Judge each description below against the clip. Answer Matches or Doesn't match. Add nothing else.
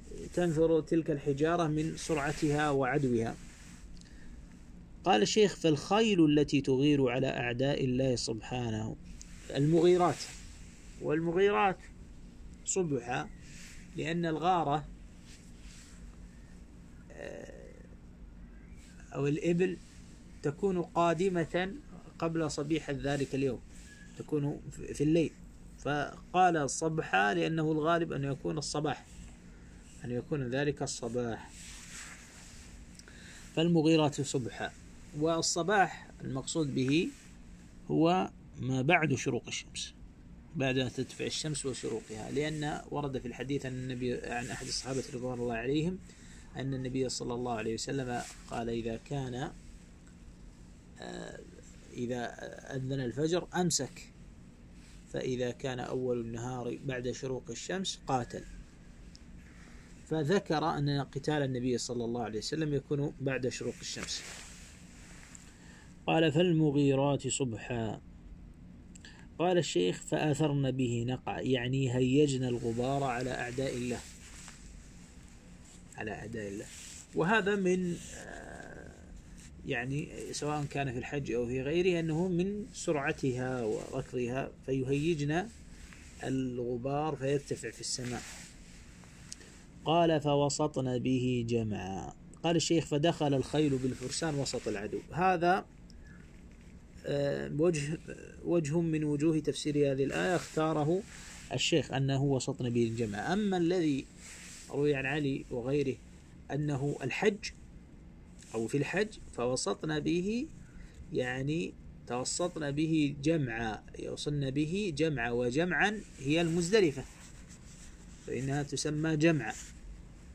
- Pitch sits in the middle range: Doesn't match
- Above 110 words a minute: Doesn't match